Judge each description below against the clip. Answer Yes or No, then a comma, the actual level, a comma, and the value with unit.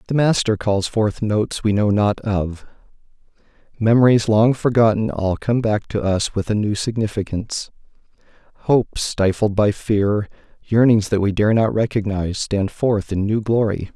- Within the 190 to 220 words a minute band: No, average, 155 wpm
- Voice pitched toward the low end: Yes, low, 105 Hz